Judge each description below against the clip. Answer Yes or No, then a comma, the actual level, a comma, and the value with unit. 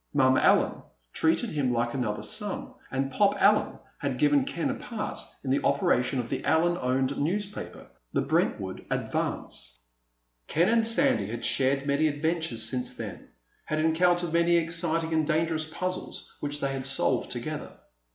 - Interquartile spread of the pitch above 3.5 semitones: Yes, average, 4.5 semitones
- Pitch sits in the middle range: Yes, medium, 155 Hz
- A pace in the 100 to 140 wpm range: No, average, 155 wpm